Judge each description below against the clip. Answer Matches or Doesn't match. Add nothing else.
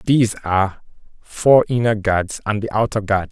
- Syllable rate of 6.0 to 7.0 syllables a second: Doesn't match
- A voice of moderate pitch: Doesn't match